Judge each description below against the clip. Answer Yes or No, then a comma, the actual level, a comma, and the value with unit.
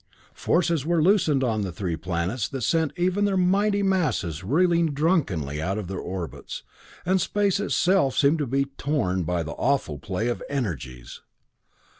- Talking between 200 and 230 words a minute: No, average, 160 wpm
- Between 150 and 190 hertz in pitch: No, low, 135 Hz